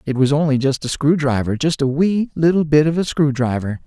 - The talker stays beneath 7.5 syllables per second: Yes, 5.5 syllables/s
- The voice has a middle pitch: Yes, medium, 145 Hz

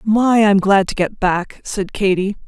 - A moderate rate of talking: Yes, average, 195 wpm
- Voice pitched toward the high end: Yes, high, 200 Hz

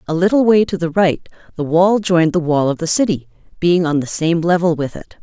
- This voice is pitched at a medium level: Yes, medium, 170 Hz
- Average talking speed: No, fast, 240 wpm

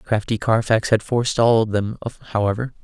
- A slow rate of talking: Yes, slow, 125 wpm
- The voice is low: Yes, low, 110 Hz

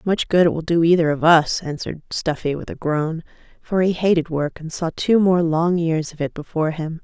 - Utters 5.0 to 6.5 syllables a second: Yes, 5.3 syllables/s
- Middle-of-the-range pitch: Yes, medium, 165 Hz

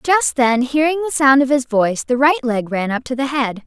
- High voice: Yes, very high, 265 Hz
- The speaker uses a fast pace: Yes, fast, 260 wpm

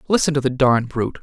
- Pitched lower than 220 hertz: Yes, low, 135 Hz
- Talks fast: Yes, fast, 245 wpm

